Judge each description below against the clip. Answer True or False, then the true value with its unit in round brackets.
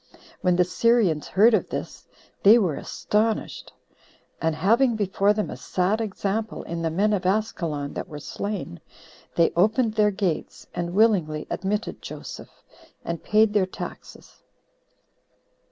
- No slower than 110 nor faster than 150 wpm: True (135 wpm)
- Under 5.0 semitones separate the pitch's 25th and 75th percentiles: True (3.9 semitones)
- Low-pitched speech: False (200 Hz)